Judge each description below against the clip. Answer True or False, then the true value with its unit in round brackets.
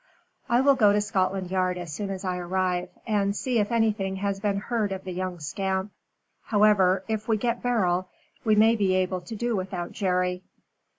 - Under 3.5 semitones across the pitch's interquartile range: True (2.6 semitones)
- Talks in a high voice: True (195 Hz)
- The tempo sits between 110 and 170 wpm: False (190 wpm)